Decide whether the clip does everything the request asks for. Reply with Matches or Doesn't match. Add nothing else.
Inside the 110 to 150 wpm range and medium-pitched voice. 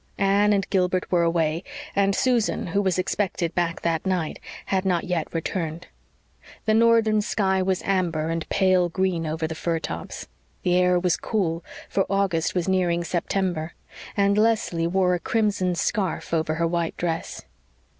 Doesn't match